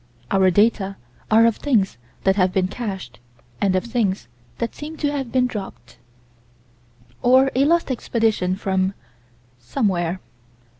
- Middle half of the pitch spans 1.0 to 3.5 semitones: No, average, 4.9 semitones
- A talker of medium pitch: No, high, 205 Hz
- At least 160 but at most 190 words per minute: No, slow, 135 wpm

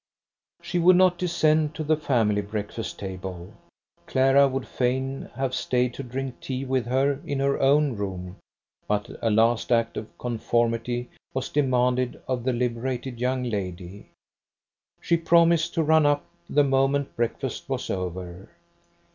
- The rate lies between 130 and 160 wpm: Yes, average, 145 wpm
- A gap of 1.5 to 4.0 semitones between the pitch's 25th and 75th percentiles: Yes, average, 3.6 semitones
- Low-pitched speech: Yes, low, 125 Hz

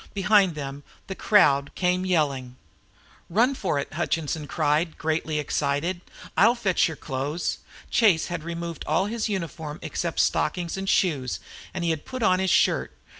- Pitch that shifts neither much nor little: Yes, average, 4.1 semitones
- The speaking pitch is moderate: Yes, medium, 170 Hz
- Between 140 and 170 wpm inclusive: Yes, average, 155 wpm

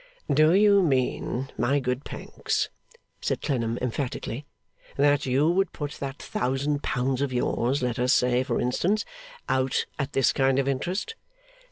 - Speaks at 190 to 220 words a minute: No, average, 150 wpm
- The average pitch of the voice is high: No, low, 135 Hz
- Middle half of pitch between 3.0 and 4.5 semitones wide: No, narrow, 2.5 semitones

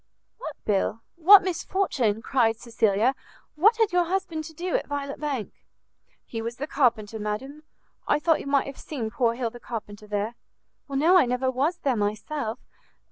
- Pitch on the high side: Yes, very high, 265 Hz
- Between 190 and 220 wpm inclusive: No, average, 170 wpm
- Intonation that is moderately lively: No, wide, 5.8 semitones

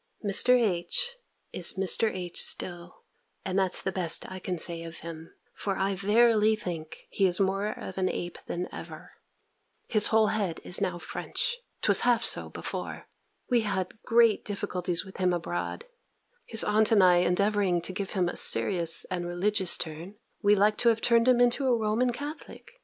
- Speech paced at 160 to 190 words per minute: Yes, average, 180 wpm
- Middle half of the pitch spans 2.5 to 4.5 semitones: Yes, average, 3.7 semitones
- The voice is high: Yes, high, 195 Hz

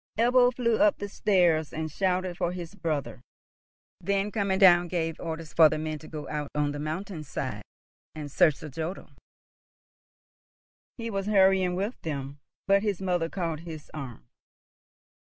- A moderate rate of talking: Yes, average, 155 wpm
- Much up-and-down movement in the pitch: No, average, 4.0 semitones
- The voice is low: No, medium, 175 Hz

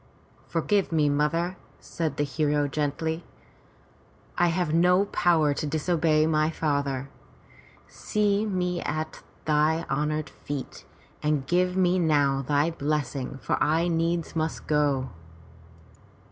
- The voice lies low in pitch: No, medium, 155 Hz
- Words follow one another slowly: Yes, slow, 120 wpm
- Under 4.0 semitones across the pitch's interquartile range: Yes, average, 2.7 semitones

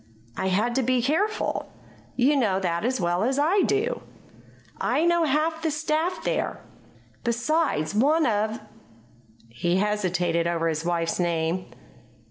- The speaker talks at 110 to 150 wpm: Yes, average, 140 wpm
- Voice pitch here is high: Yes, high, 220 Hz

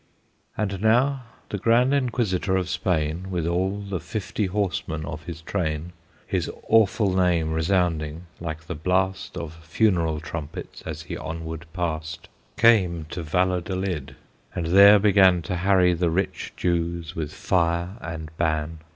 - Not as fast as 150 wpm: Yes, average, 140 wpm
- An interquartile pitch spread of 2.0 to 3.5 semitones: Yes, average, 2.9 semitones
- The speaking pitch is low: Yes, very low, 90 Hz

